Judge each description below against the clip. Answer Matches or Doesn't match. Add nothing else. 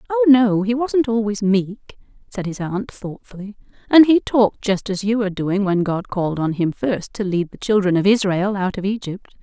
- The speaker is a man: Doesn't match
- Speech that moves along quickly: Matches